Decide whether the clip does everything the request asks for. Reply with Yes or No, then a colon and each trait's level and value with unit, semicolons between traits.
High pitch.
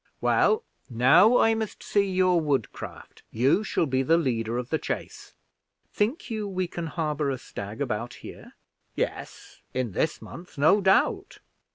No: medium, 160 Hz